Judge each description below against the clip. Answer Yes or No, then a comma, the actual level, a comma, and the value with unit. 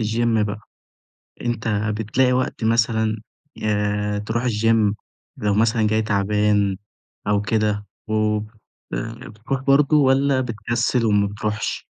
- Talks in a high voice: No, low, 110 Hz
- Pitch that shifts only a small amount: Yes, narrow, 2.1 semitones